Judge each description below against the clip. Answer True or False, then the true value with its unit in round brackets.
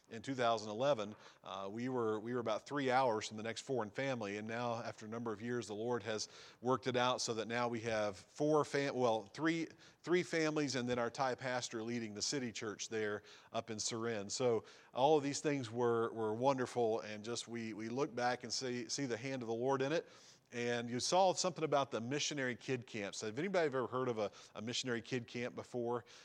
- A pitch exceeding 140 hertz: False (120 Hz)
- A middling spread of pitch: True (3.1 semitones)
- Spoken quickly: True (220 wpm)